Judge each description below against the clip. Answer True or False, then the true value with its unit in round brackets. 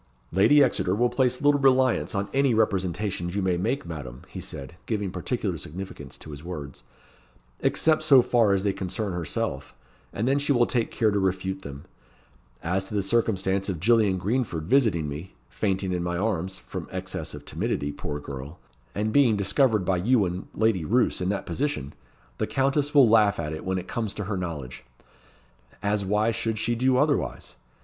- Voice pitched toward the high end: False (100 Hz)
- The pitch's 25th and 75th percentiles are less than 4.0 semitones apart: False (5.1 semitones)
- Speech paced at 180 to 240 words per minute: True (185 wpm)